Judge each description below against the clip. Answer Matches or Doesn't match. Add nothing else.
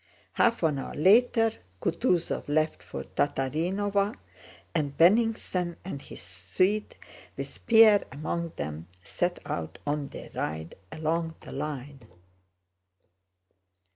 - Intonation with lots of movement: Matches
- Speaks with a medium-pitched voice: Matches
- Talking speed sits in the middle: Doesn't match